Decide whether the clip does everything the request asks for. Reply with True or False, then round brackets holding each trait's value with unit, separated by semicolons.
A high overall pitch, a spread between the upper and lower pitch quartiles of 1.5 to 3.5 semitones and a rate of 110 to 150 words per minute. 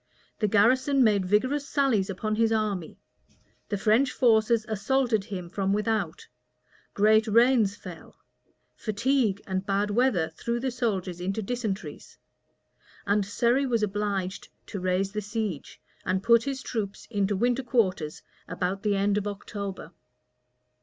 True (210 Hz; 3.2 semitones; 135 wpm)